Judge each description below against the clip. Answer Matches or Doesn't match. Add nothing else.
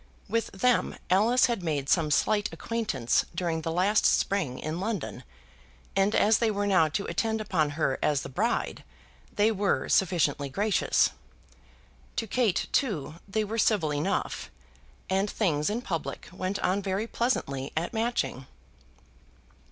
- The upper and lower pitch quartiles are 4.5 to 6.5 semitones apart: Matches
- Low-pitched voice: Doesn't match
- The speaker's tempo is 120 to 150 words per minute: Matches